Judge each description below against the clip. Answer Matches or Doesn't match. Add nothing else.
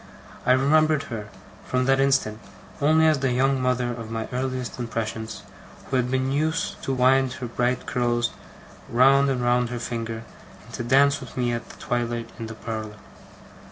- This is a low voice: Matches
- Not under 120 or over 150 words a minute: Doesn't match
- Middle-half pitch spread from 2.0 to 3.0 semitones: Matches